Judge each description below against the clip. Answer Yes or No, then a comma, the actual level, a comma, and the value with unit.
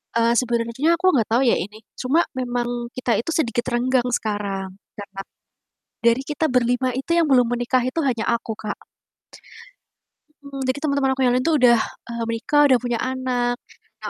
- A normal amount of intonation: No, narrow, 2.2 semitones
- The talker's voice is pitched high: Yes, high, 245 Hz